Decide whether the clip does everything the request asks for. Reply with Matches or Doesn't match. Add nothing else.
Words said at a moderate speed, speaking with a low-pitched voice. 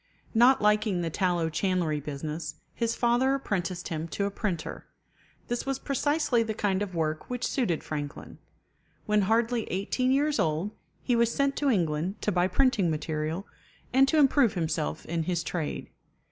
Doesn't match